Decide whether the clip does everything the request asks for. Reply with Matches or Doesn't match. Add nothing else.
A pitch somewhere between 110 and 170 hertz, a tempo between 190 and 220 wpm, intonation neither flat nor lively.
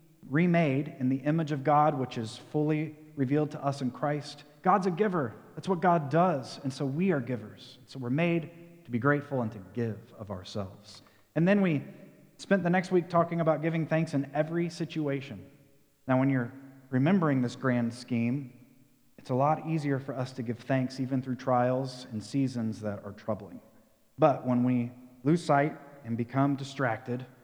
Doesn't match